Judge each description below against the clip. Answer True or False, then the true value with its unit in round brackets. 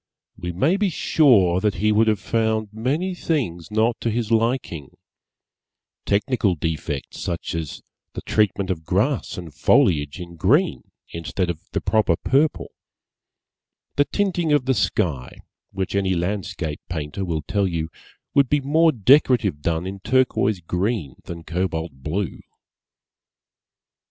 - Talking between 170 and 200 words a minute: False (135 wpm)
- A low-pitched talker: True (100 Hz)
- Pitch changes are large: True (6.5 semitones)